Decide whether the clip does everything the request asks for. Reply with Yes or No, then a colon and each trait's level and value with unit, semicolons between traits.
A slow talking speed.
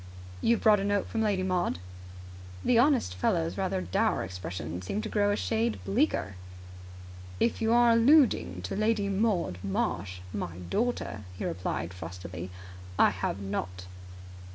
No: average, 150 wpm